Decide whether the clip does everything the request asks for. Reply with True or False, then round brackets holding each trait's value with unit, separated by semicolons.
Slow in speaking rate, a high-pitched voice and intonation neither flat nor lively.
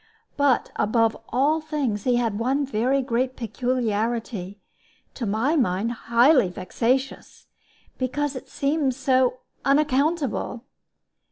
True (105 wpm; 255 Hz; 3.3 semitones)